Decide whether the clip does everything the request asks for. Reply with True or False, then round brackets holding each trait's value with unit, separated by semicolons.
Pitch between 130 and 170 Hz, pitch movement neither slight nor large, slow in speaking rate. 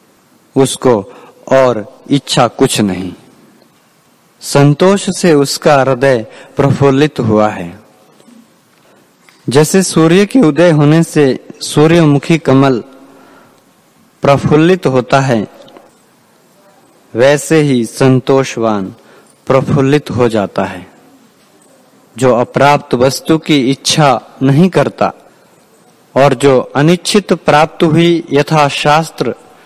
True (140 Hz; 3.7 semitones; 90 wpm)